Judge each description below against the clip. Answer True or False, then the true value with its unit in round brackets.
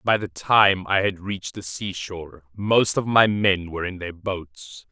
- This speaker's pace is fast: False (195 wpm)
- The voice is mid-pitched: False (95 Hz)